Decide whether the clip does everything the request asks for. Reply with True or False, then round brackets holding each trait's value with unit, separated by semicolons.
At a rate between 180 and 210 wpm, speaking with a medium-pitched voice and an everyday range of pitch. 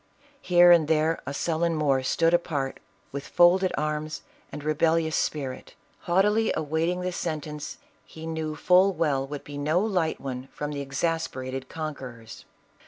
False (150 wpm; 155 Hz; 3.1 semitones)